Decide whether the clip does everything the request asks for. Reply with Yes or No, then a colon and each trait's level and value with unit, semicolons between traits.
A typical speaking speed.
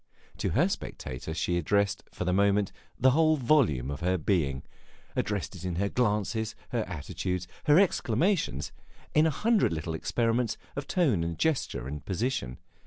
Yes: average, 160 wpm